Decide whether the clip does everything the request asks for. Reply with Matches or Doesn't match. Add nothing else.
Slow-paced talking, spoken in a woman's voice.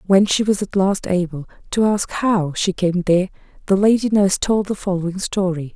Doesn't match